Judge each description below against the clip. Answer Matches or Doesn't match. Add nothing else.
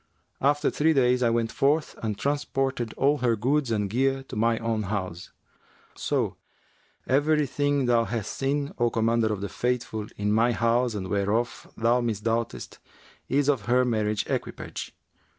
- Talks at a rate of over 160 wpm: Doesn't match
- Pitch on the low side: Matches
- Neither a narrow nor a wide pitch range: Matches